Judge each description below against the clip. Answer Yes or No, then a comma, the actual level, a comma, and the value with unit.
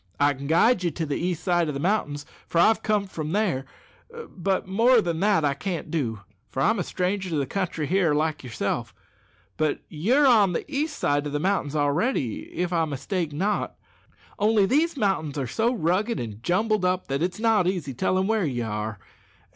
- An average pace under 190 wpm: No, average, 195 wpm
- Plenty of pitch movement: Yes, wide, 5.9 semitones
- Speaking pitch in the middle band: Yes, medium, 175 Hz